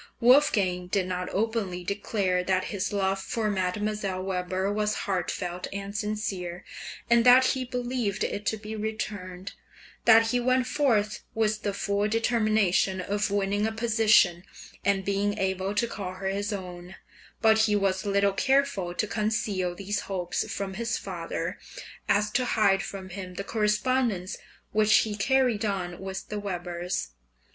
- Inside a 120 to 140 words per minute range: No, average, 150 wpm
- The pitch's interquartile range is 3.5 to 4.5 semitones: No, narrow, 2.6 semitones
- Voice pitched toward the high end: Yes, high, 205 Hz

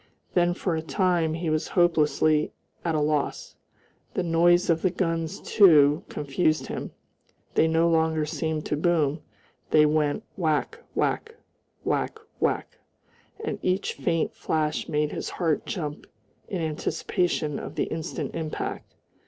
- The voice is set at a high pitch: No, medium, 160 Hz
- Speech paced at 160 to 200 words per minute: No, slow, 135 wpm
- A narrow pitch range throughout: Yes, narrow, 2.3 semitones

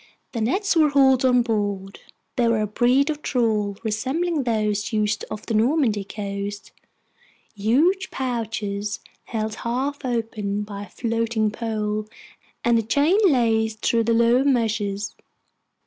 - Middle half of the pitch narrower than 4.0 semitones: Yes, average, 3.4 semitones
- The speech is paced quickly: No, slow, 135 wpm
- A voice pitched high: Yes, high, 225 Hz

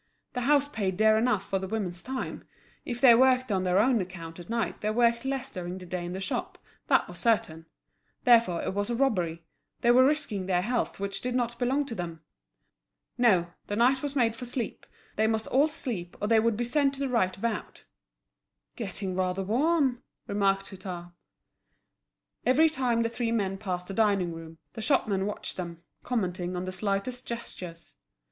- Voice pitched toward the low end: No, high, 215 Hz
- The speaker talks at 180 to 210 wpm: Yes, average, 190 wpm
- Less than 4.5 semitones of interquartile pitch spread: No, average, 5.0 semitones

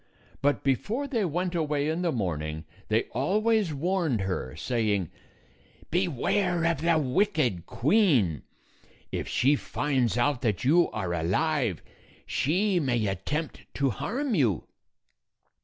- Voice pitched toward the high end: No, medium, 145 Hz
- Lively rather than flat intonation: Yes, wide, 8.0 semitones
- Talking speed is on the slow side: Yes, slow, 125 wpm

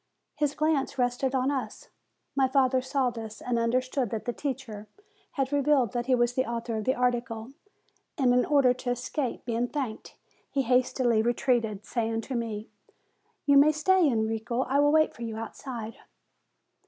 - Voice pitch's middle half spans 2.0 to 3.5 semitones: Yes, average, 2.8 semitones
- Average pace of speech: Yes, average, 170 wpm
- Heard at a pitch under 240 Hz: No, very high, 250 Hz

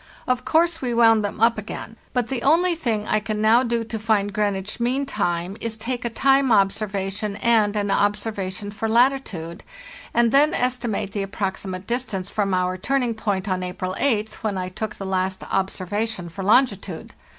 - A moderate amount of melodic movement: Yes, average, 3.5 semitones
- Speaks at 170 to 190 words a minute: Yes, average, 180 wpm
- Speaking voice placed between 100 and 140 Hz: No, high, 215 Hz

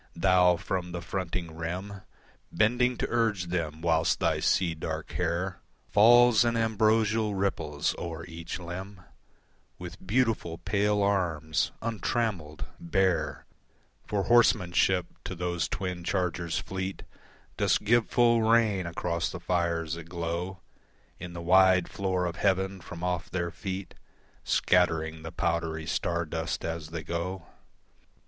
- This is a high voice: No, very low, 90 Hz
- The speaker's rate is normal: No, slow, 130 wpm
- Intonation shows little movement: No, average, 3.1 semitones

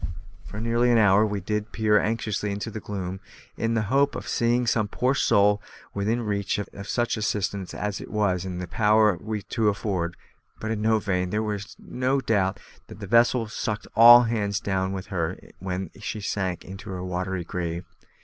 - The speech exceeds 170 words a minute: Yes, average, 180 wpm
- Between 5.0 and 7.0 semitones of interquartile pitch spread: No, average, 2.8 semitones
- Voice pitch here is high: No, low, 105 Hz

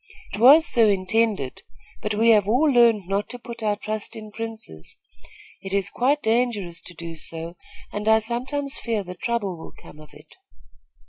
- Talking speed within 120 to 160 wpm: No, average, 180 wpm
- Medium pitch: No, high, 215 Hz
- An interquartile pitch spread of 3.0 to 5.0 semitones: Yes, average, 3.6 semitones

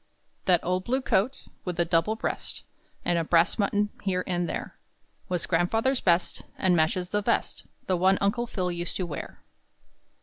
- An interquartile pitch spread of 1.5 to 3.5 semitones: Yes, average, 2.8 semitones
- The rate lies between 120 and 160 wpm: No, average, 170 wpm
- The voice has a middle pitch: Yes, medium, 180 Hz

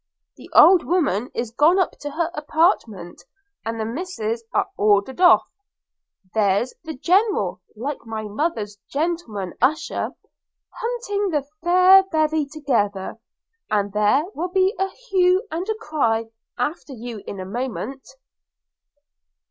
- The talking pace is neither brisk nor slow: No, slow, 125 wpm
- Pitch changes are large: Yes, wide, 8.3 semitones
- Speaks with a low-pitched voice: No, very high, 285 Hz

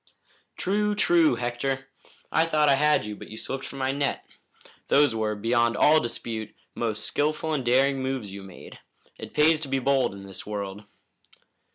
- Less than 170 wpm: No, average, 175 wpm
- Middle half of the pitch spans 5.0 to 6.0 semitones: Yes, wide, 5.4 semitones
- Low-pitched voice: Yes, low, 130 Hz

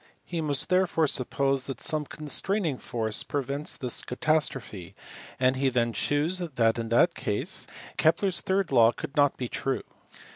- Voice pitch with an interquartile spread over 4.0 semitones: Yes, average, 4.4 semitones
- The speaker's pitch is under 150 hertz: Yes, medium, 140 Hz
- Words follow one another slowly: No, average, 155 wpm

